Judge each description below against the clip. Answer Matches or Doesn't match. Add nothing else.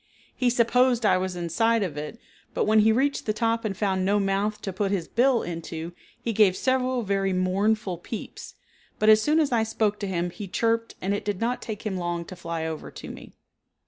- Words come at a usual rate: Doesn't match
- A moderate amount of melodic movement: Matches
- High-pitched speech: Matches